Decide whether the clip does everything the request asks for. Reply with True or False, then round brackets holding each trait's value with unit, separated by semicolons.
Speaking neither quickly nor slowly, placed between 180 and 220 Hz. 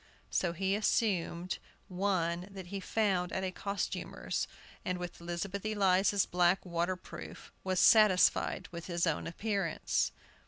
False (125 wpm; 185 Hz)